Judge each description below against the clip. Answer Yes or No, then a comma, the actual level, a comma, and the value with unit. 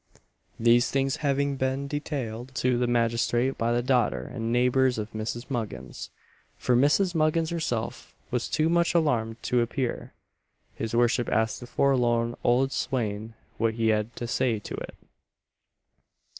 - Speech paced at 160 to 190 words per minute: No, average, 145 wpm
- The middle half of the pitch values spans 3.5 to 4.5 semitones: No, average, 2.9 semitones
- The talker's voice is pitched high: No, low, 120 Hz